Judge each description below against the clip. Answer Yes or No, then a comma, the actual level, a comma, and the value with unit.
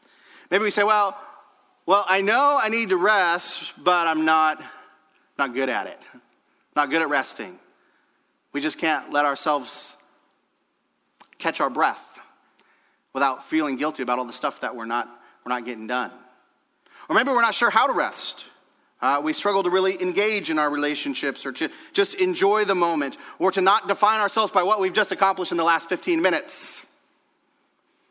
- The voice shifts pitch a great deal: Yes, wide, 8.1 semitones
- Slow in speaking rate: No, average, 175 wpm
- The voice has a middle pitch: No, high, 195 Hz